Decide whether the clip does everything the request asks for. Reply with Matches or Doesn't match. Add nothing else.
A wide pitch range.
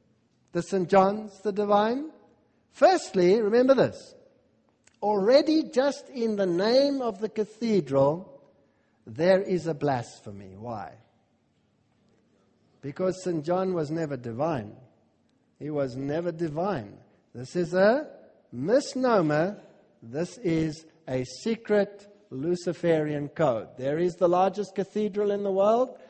Matches